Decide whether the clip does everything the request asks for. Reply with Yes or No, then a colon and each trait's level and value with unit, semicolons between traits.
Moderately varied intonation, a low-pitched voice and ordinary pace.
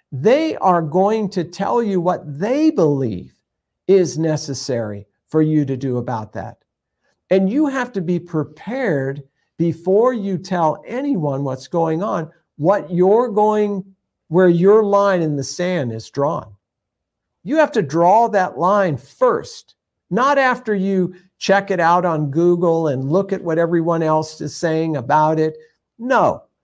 No: average, 4.9 semitones; medium, 175 Hz; average, 150 wpm